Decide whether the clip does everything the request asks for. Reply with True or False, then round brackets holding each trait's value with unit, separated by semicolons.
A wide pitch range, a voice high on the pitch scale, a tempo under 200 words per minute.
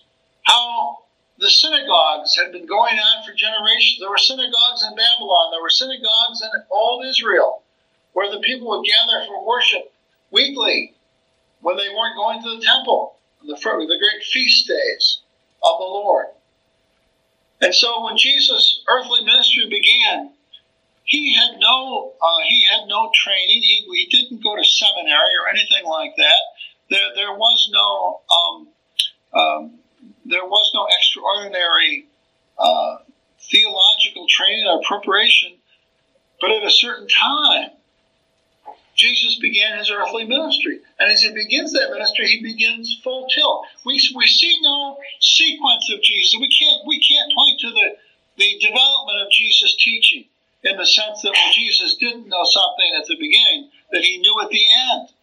True (5.9 semitones; 240 Hz; 155 wpm)